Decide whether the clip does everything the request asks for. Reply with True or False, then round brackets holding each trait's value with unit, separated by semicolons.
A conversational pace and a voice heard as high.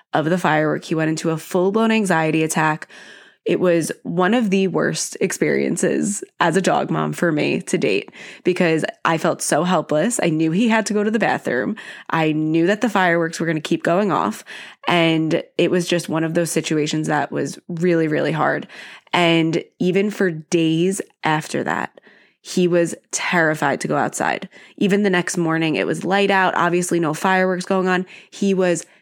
False (185 wpm; 170 Hz)